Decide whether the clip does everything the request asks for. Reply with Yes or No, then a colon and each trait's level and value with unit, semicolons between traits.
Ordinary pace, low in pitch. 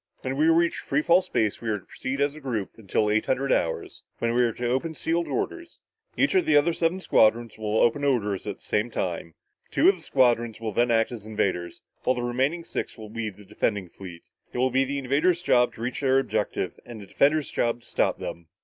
No: fast, 235 wpm; low, 120 Hz